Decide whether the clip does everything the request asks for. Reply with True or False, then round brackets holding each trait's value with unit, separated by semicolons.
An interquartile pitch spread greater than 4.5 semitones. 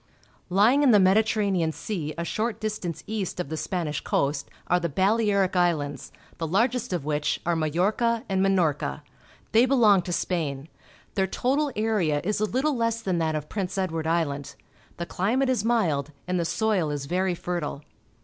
True (5.2 semitones)